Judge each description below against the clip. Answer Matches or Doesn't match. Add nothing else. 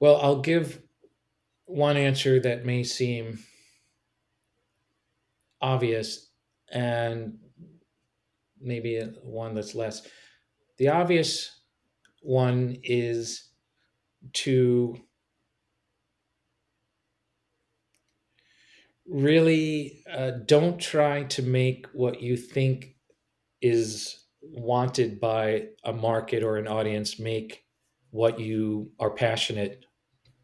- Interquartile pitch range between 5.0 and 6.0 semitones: Doesn't match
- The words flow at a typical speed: Doesn't match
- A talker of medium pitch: Doesn't match